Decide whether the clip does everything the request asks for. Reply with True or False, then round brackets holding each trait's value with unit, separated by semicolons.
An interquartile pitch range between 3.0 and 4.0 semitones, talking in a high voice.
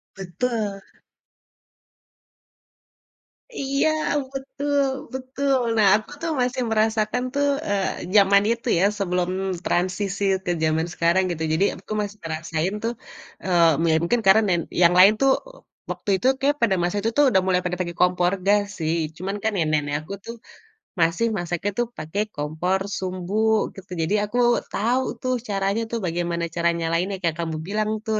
False (4.6 semitones; 195 Hz)